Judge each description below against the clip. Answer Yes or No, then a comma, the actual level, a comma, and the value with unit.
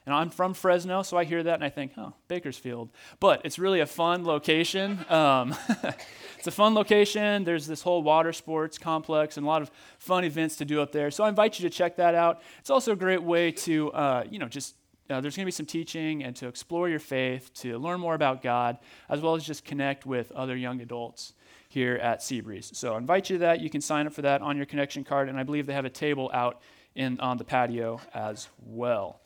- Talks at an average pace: No, fast, 240 wpm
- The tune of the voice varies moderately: Yes, average, 4.7 semitones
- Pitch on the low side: No, medium, 150 Hz